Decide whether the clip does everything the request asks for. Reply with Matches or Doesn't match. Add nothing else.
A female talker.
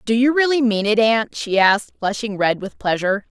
Matches